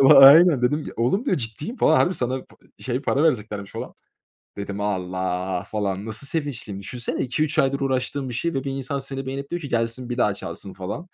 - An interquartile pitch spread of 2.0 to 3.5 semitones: No, average, 5.2 semitones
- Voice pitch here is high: No, low, 130 Hz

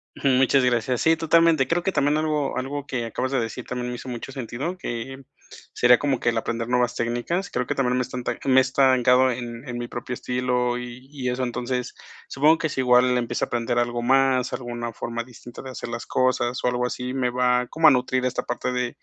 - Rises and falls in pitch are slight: Yes, narrow, 1.6 semitones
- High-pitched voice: No, low, 125 Hz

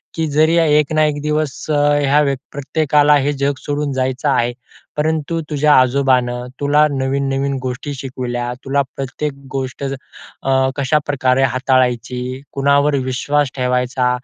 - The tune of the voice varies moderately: No, narrow, 2.2 semitones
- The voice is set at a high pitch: No, medium, 140 Hz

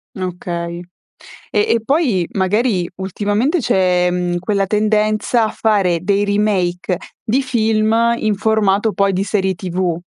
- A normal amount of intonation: Yes, average, 3.1 semitones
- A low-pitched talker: No, high, 200 Hz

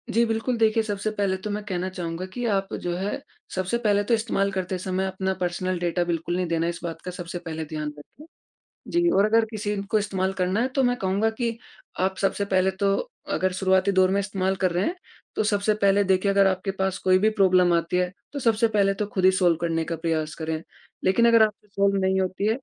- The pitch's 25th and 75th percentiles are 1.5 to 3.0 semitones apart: Yes, narrow, 2.4 semitones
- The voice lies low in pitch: No, high, 190 Hz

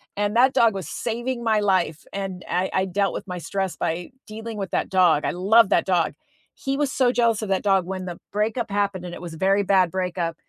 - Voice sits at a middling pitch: No, high, 195 Hz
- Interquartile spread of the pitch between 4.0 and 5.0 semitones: No, average, 3.4 semitones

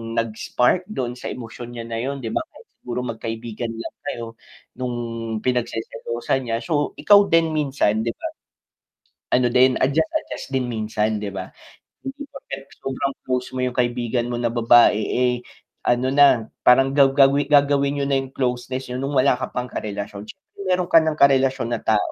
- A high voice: No, low, 125 Hz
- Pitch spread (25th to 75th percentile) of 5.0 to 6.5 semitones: No, average, 3.0 semitones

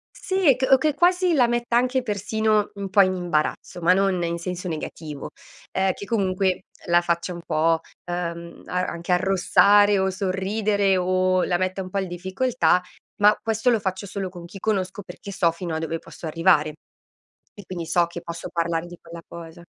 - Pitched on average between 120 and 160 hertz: No, medium, 185 Hz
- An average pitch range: Yes, average, 3.0 semitones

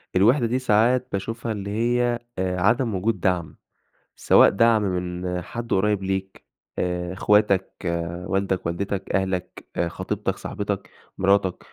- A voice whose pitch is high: No, low, 100 Hz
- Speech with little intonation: No, average, 3.6 semitones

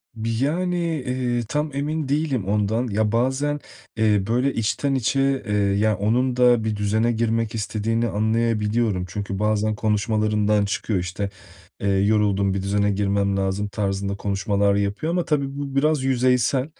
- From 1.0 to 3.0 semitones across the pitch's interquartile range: No, average, 3.8 semitones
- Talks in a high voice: No, low, 110 Hz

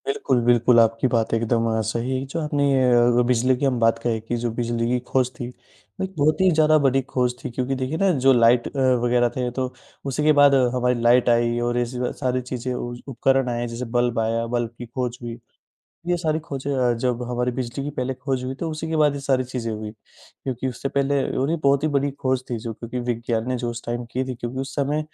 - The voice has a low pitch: Yes, low, 125 Hz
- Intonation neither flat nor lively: No, narrow, 2.3 semitones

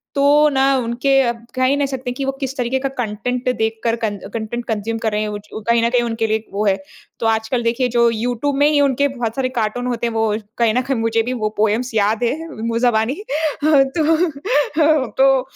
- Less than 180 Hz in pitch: No, high, 240 Hz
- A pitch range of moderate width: Yes, average, 3.3 semitones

